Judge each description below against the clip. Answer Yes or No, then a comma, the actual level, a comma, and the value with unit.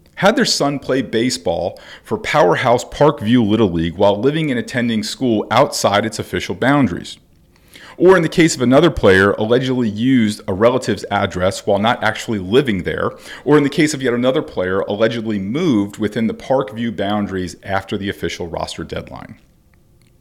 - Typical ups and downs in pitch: Yes, average, 4.5 semitones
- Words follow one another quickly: No, average, 165 wpm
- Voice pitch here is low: Yes, low, 115 Hz